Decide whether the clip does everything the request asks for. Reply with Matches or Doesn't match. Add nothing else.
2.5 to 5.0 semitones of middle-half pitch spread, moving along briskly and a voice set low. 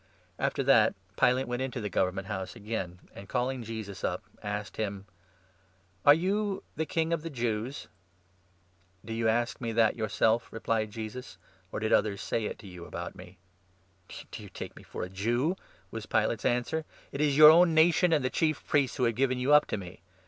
Doesn't match